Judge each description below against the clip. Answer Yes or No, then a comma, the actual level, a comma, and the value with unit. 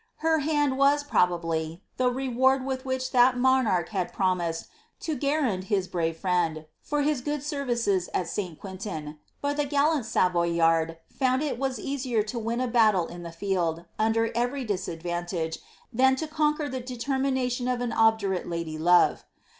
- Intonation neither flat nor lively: No, wide, 7.1 semitones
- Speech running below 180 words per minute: Yes, average, 165 wpm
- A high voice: Yes, high, 230 Hz